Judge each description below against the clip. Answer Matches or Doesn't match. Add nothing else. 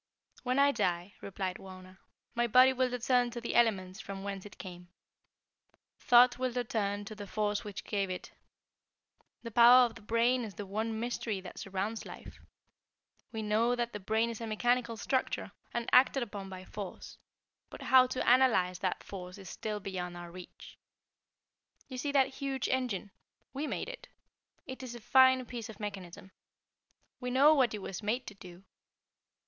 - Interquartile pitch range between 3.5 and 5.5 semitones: Matches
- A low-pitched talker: Doesn't match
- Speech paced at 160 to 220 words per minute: Matches